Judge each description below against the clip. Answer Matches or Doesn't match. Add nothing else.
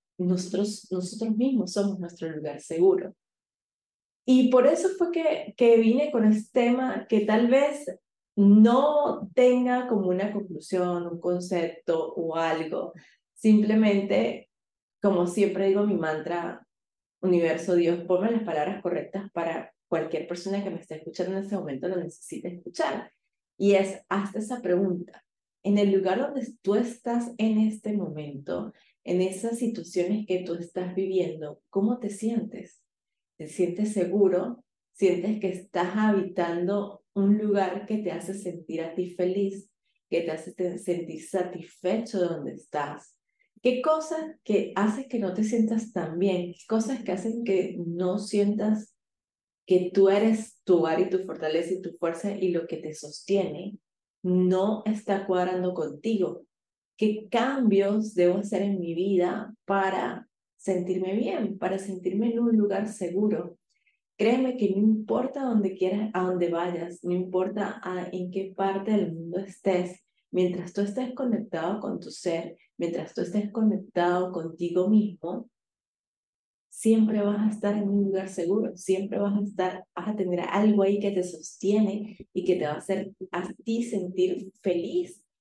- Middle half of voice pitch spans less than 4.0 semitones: Matches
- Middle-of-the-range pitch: Doesn't match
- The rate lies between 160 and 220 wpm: Doesn't match